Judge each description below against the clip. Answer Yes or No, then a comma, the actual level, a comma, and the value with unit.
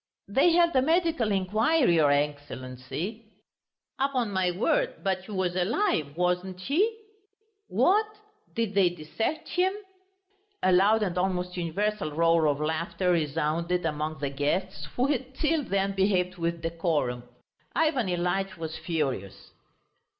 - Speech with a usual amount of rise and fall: No, wide, 5.8 semitones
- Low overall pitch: No, medium, 185 Hz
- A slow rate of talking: Yes, slow, 130 wpm